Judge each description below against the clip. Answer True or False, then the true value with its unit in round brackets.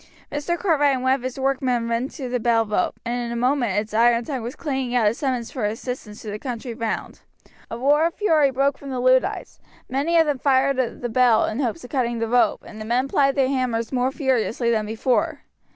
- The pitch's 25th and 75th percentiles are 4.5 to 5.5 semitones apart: False (2.8 semitones)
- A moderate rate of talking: False (230 wpm)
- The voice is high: True (250 Hz)